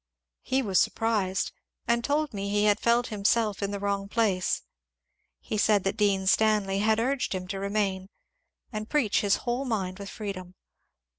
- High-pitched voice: Yes, high, 205 Hz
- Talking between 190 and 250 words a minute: No, average, 165 wpm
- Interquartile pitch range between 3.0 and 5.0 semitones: No, narrow, 2.5 semitones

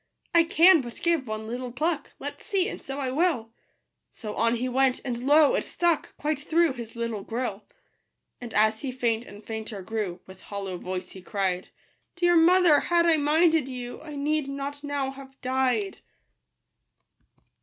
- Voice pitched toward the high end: Yes, very high, 265 Hz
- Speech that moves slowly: No, average, 175 wpm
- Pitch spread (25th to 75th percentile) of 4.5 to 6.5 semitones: Yes, wide, 5.6 semitones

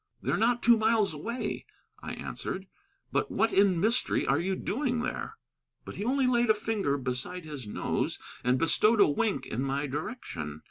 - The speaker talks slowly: No, average, 175 wpm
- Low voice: No, high, 200 Hz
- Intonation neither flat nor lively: No, wide, 8.3 semitones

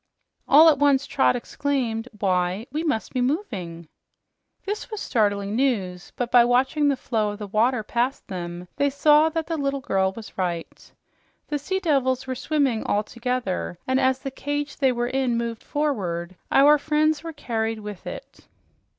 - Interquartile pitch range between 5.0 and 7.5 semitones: Yes, wide, 5.5 semitones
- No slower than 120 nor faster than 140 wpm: No, average, 170 wpm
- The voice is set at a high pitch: Yes, very high, 250 Hz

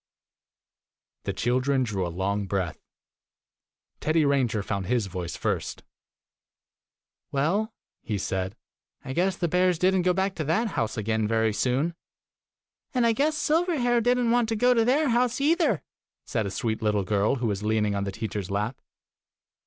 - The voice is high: No, low, 130 Hz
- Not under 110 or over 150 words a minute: No, average, 175 wpm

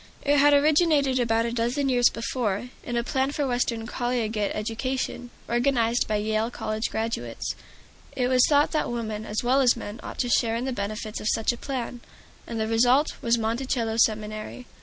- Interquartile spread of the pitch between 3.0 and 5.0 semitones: No, narrow, 2.6 semitones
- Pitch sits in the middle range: No, high, 235 Hz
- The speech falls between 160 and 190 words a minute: Yes, average, 180 wpm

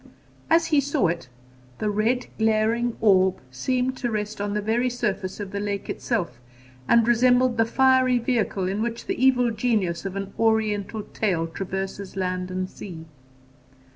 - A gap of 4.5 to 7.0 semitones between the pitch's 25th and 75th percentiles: No, average, 4.0 semitones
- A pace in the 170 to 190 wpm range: No, average, 160 wpm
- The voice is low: No, high, 215 Hz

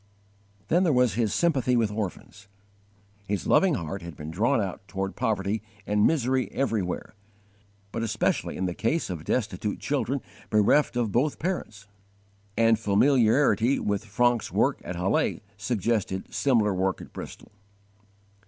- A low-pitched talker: Yes, low, 110 Hz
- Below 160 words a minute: Yes, slow, 135 wpm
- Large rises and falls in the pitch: No, average, 4.2 semitones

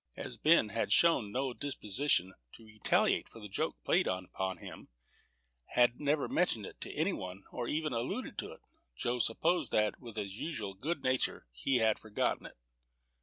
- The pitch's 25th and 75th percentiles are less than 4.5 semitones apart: No, average, 5.2 semitones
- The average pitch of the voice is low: Yes, low, 115 Hz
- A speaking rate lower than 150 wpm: No, average, 170 wpm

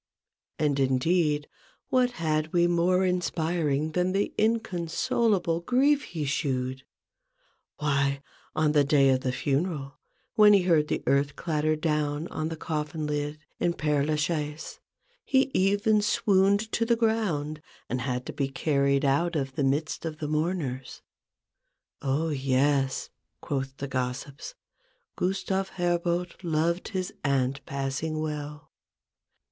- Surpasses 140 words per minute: No, slow, 135 wpm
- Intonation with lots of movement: No, average, 4.2 semitones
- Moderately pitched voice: Yes, medium, 155 Hz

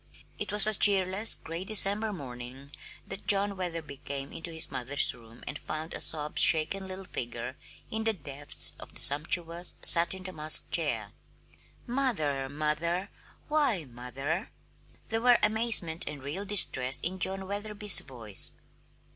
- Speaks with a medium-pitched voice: Yes, medium, 170 Hz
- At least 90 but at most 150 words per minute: Yes, average, 140 wpm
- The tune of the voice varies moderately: No, wide, 6.1 semitones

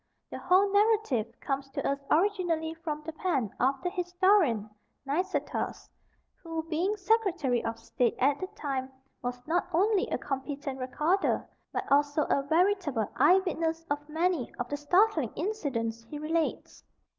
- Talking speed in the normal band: Yes, average, 145 wpm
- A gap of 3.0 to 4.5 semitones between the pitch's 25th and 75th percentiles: No, average, 5.1 semitones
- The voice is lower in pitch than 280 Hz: No, very high, 315 Hz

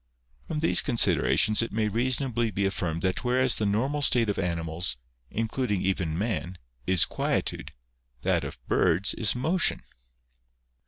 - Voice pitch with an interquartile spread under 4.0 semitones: No, average, 4.9 semitones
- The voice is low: Yes, low, 110 Hz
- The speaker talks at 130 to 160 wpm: Yes, average, 140 wpm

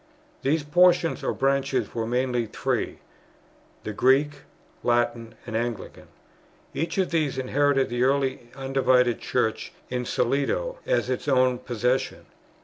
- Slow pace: Yes, slow, 125 wpm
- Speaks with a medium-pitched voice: No, low, 130 Hz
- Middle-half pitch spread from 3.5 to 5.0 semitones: No, average, 2.8 semitones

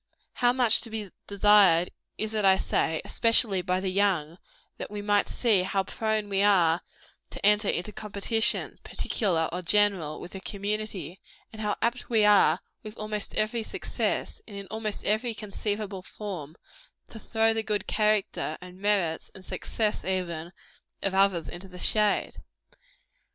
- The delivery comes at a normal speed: Yes, average, 155 wpm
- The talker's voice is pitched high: Yes, high, 205 Hz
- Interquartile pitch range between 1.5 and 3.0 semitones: Yes, narrow, 2.5 semitones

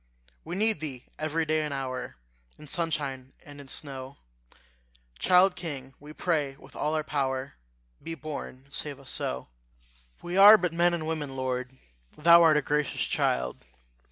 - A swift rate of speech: No, average, 160 wpm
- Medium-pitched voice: Yes, medium, 150 Hz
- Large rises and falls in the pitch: No, average, 3.6 semitones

